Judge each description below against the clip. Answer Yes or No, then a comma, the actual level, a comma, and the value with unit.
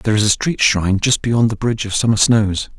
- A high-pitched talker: No, low, 110 Hz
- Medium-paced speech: No, fast, 260 wpm